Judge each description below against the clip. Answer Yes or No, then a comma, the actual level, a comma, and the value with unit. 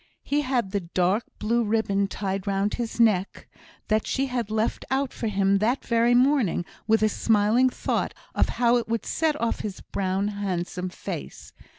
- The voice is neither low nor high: No, high, 215 Hz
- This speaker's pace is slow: No, average, 175 wpm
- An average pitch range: Yes, average, 3.3 semitones